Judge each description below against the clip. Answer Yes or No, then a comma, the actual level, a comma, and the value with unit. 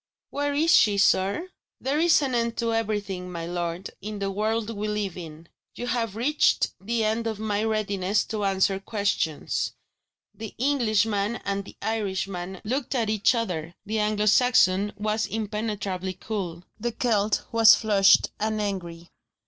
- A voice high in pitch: Yes, high, 210 Hz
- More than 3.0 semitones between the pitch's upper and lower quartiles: No, average, 2.7 semitones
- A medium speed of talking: Yes, average, 155 wpm